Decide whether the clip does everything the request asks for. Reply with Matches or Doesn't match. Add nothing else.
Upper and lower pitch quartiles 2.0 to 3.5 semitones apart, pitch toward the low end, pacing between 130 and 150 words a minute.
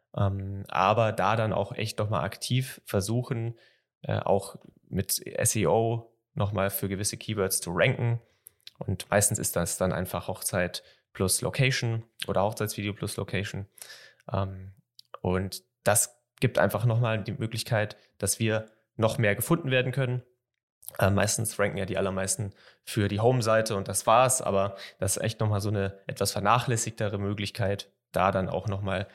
Matches